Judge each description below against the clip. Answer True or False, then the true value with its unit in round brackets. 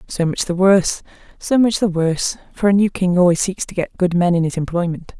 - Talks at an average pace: False (245 wpm)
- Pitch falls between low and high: True (180 Hz)